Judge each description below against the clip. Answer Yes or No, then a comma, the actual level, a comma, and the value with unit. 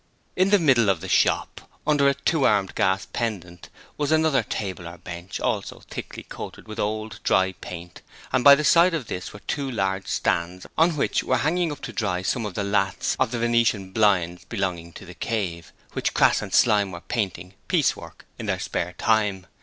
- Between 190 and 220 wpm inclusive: Yes, average, 195 wpm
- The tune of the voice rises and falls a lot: Yes, wide, 6.1 semitones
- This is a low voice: Yes, low, 105 Hz